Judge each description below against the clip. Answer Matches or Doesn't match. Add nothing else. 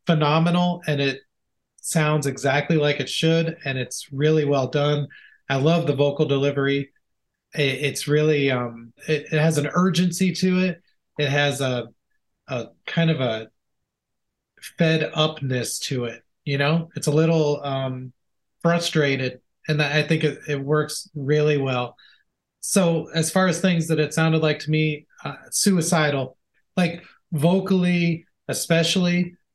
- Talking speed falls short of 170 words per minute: Matches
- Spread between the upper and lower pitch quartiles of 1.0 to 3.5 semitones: Matches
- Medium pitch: Matches